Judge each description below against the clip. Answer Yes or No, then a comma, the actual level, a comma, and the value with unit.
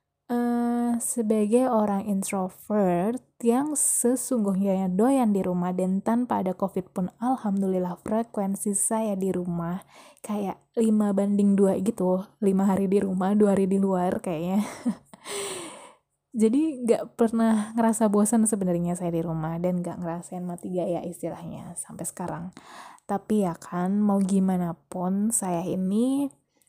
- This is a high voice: Yes, high, 200 Hz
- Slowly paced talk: No, average, 135 wpm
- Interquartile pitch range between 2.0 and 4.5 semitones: Yes, average, 3.7 semitones